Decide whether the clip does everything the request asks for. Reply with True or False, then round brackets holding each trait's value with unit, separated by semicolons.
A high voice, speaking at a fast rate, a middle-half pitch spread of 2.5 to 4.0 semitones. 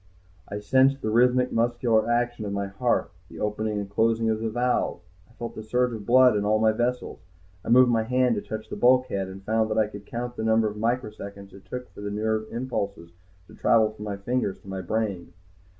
False (110 Hz; 220 wpm; 2.8 semitones)